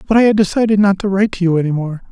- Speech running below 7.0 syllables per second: No, 8.0 syllables/s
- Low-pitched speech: No, high, 195 Hz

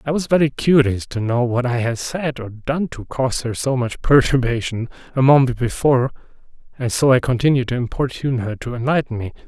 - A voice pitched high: No, low, 130 Hz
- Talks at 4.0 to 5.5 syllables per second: No, 5.7 syllables/s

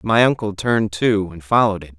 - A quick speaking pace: Yes, fast, 210 wpm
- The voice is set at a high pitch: No, low, 105 Hz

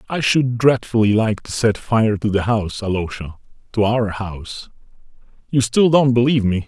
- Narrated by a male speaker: Yes, male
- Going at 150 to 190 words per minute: Yes, average, 170 wpm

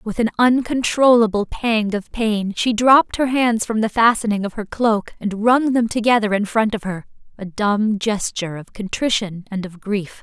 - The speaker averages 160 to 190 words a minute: Yes, average, 180 wpm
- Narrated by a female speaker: Yes, female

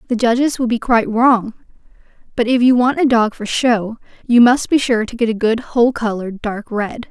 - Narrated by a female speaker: Yes, female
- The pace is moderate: No, fast, 220 wpm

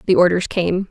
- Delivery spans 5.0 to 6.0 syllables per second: Yes, 5.3 syllables/s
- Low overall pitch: No, medium, 180 Hz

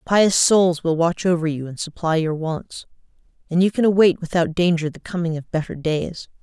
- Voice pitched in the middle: Yes, medium, 170 Hz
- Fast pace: No, average, 195 wpm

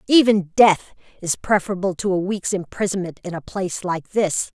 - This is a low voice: No, high, 190 Hz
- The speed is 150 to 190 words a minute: Yes, average, 170 wpm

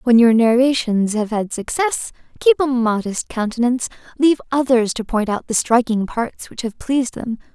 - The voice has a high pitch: Yes, high, 240 Hz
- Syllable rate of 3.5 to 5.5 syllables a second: Yes, 5.0 syllables/s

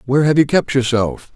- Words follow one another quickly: Yes, fast, 220 wpm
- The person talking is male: Yes, male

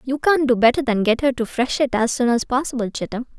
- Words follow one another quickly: Yes, fast, 250 wpm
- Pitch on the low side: No, very high, 250 Hz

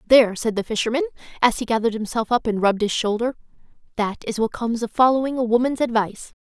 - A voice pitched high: Yes, high, 230 Hz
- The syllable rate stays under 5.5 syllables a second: No, 7.0 syllables/s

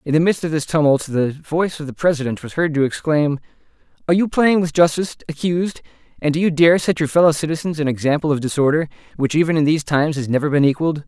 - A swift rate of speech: Yes, fast, 220 wpm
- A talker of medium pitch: Yes, medium, 155 Hz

